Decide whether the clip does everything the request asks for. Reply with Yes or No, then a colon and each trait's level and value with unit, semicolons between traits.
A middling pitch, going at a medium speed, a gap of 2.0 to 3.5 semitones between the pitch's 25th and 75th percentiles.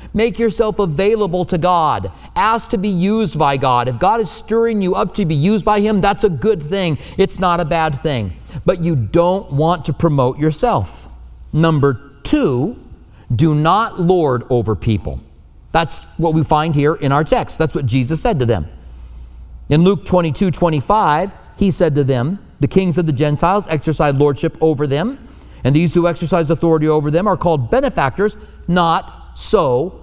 No: medium, 165 Hz; average, 175 wpm; average, 5.2 semitones